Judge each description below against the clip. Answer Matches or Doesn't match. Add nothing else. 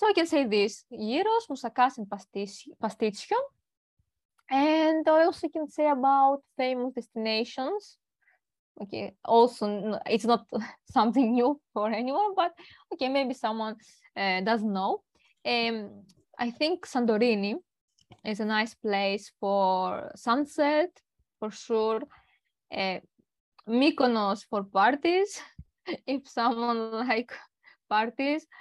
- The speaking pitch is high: Matches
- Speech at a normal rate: Doesn't match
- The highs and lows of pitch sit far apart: Matches